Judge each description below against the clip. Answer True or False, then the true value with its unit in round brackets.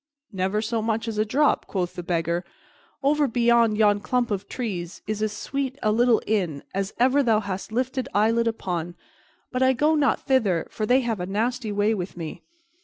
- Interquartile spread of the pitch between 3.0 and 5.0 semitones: True (4.1 semitones)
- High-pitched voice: True (220 Hz)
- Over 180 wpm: True (190 wpm)